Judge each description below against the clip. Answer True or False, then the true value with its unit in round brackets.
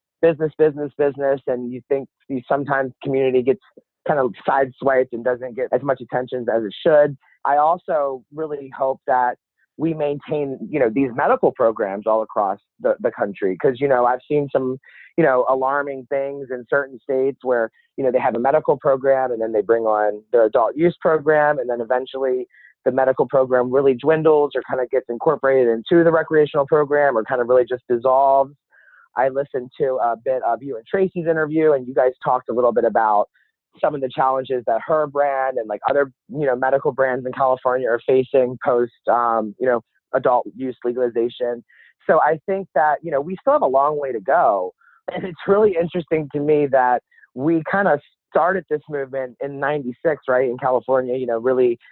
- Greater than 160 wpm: True (195 wpm)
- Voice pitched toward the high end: False (135 Hz)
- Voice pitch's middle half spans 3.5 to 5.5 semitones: False (2.9 semitones)